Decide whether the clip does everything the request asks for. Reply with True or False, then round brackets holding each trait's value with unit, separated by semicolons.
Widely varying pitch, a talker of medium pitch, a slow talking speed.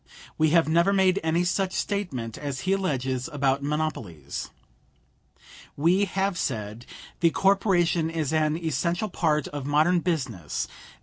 False (4.7 semitones; 160 Hz; 130 wpm)